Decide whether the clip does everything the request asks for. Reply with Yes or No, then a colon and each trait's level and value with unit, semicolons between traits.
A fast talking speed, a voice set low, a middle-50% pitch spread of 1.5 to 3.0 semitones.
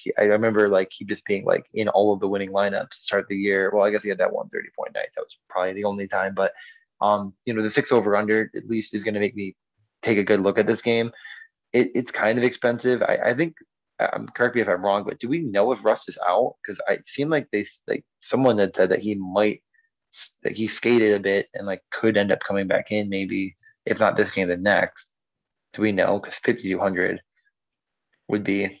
Yes: fast, 240 wpm; low, 105 Hz; narrow, 2.4 semitones